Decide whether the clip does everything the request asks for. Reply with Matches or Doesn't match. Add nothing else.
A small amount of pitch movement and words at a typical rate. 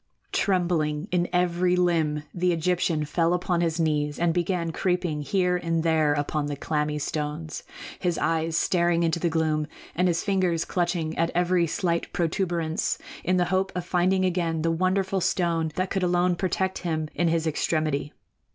Matches